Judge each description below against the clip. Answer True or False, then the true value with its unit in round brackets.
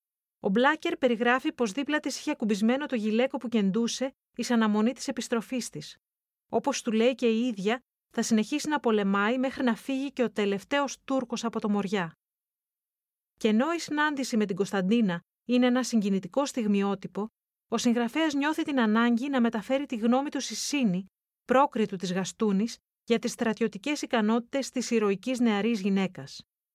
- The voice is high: True (235 Hz)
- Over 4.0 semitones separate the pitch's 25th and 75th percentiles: False (3.5 semitones)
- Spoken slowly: False (155 wpm)